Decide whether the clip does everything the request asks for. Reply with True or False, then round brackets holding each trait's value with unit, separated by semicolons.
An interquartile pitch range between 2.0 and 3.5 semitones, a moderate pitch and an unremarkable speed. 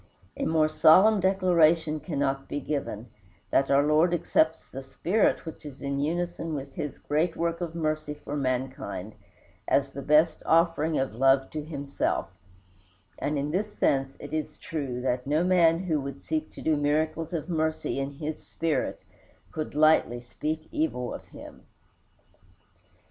True (2.9 semitones; 155 Hz; 155 wpm)